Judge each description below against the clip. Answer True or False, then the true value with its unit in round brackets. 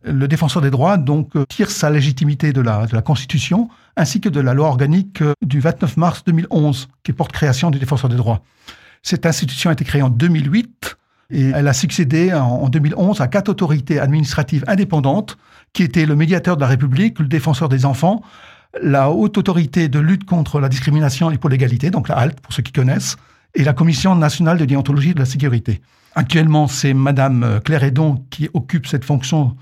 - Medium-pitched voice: True (150 Hz)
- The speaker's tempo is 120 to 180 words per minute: False (195 wpm)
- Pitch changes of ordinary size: True (3.6 semitones)